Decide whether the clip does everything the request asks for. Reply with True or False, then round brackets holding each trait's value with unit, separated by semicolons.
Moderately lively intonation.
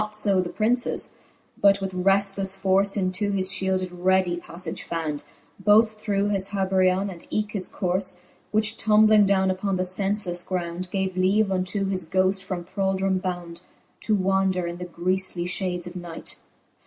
False (1.5 semitones)